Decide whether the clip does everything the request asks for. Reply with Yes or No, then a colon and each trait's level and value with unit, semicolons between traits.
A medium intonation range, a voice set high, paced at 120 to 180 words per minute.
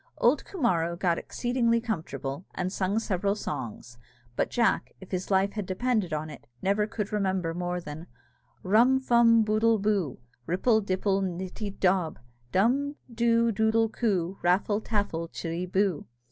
Yes: average, 4.1 semitones; high, 200 Hz; slow, 135 wpm